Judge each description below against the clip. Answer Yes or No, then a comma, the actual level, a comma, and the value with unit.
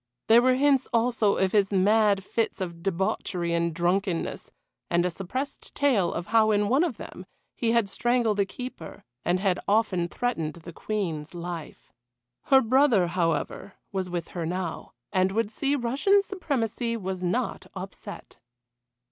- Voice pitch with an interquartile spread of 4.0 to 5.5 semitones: Yes, average, 5.1 semitones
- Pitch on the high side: Yes, high, 200 Hz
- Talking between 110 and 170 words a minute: Yes, average, 155 wpm